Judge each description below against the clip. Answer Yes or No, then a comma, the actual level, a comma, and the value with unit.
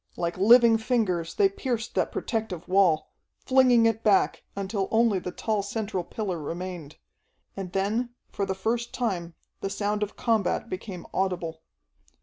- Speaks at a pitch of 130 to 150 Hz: No, high, 200 Hz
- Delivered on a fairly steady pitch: No, average, 3.8 semitones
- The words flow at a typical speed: Yes, average, 145 wpm